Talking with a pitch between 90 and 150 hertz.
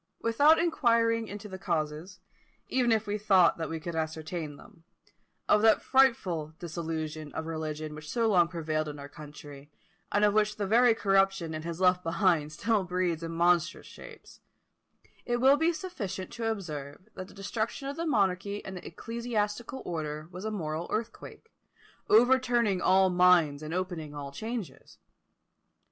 No: medium, 185 Hz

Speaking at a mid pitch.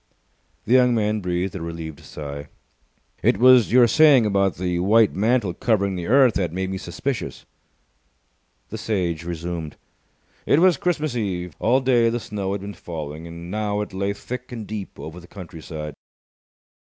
No: low, 100 Hz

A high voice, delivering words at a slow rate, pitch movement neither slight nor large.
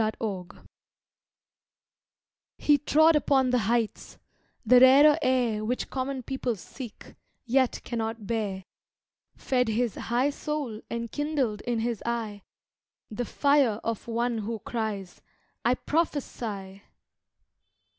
Yes: high, 235 Hz; slow, 115 wpm; average, 3.4 semitones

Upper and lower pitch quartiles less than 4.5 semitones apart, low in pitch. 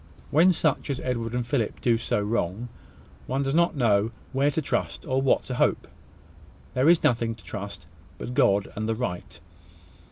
Yes: average, 4.1 semitones; low, 120 Hz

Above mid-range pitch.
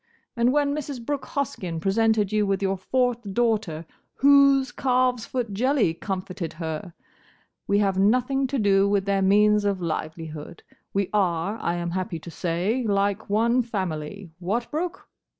Yes: high, 205 Hz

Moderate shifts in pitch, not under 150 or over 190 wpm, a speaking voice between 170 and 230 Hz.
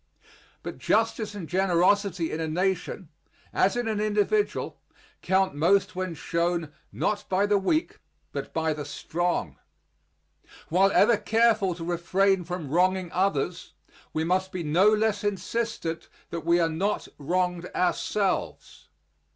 No: average, 3.3 semitones; slow, 135 wpm; medium, 185 Hz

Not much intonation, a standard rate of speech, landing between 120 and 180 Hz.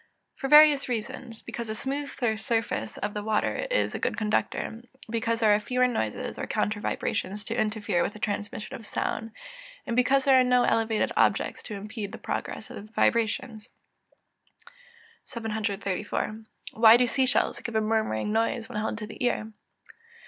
No: narrow, 2.3 semitones; average, 170 wpm; high, 220 Hz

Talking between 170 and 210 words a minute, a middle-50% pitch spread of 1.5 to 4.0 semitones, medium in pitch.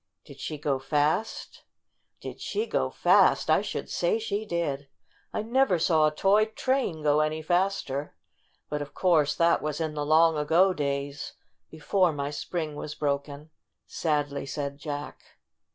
No: average, 150 wpm; average, 3.5 semitones; medium, 155 Hz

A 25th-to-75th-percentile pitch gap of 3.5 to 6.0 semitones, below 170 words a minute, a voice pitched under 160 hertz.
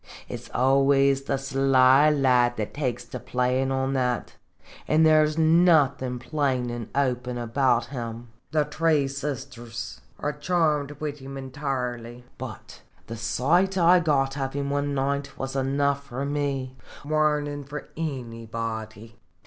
No: average, 2.8 semitones; average, 140 wpm; low, 135 Hz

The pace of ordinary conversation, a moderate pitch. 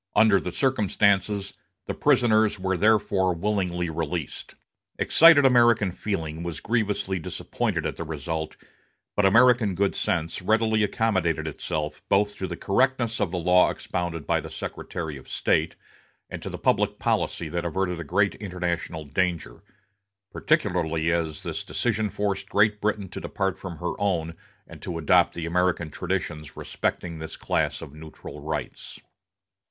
No: average, 145 wpm; very low, 90 Hz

